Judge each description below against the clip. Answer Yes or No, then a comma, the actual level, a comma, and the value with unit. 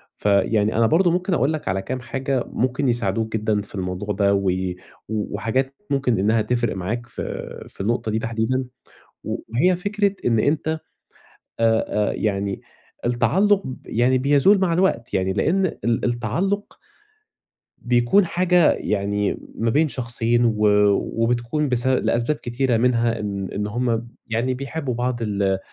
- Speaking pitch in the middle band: No, low, 120 Hz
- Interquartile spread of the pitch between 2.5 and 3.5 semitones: No, average, 4.4 semitones